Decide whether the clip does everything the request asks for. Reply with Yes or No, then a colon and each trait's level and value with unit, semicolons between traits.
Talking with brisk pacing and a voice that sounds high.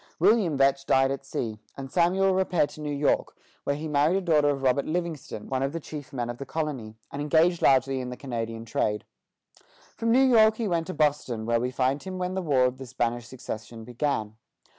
No: fast, 215 wpm; medium, 140 Hz